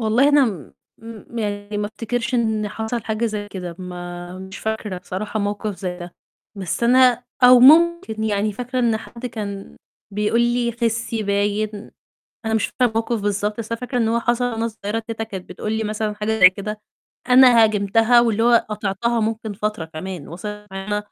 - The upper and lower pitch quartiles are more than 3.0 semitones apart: No, narrow, 2.4 semitones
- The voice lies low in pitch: No, high, 215 Hz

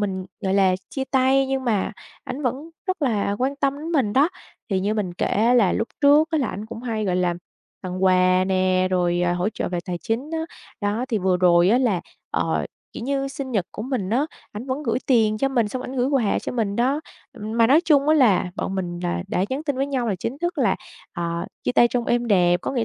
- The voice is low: No, high, 225 Hz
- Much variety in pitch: Yes, wide, 6.2 semitones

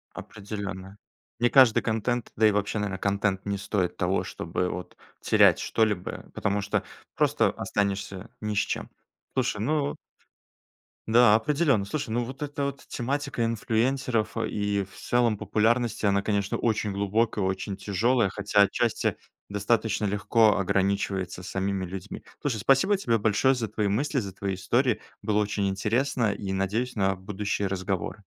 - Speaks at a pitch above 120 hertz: No, low, 105 Hz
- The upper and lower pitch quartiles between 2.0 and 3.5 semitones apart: Yes, average, 3.2 semitones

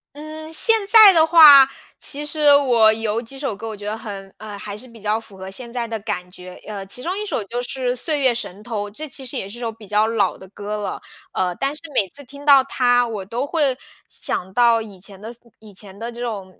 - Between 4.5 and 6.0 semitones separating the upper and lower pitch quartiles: Yes, average, 4.9 semitones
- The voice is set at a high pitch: Yes, high, 230 Hz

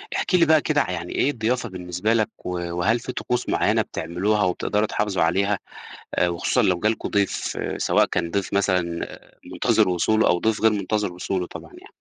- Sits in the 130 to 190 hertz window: No, low, 100 Hz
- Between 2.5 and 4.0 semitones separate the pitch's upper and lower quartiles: Yes, average, 3.7 semitones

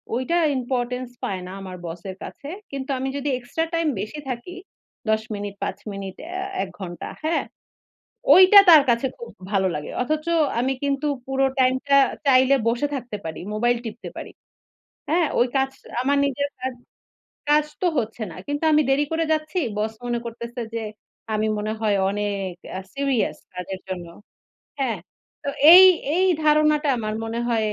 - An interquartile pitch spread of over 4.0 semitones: Yes, average, 5.1 semitones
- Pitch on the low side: No, very high, 250 Hz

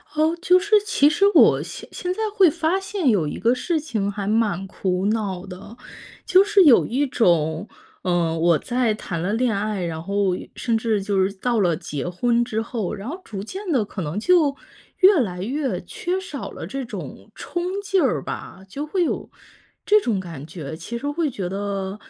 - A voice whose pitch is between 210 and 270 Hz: Yes, high, 225 Hz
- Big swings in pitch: Yes, wide, 8.6 semitones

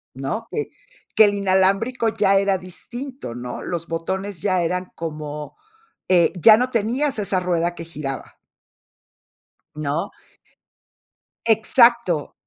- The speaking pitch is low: No, high, 190 Hz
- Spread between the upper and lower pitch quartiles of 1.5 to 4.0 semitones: No, average, 5.0 semitones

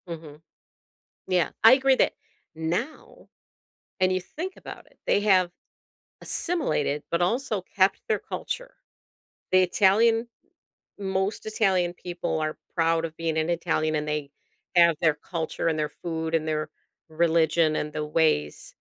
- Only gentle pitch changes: No, average, 3.5 semitones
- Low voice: No, medium, 170 Hz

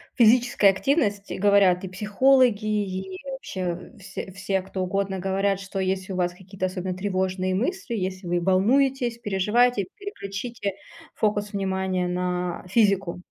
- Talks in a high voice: Yes, high, 195 Hz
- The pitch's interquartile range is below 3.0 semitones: Yes, narrow, 2.4 semitones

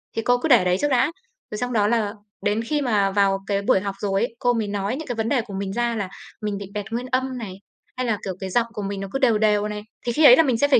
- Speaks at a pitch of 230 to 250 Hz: No, high, 220 Hz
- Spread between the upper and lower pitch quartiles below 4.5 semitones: Yes, average, 3.5 semitones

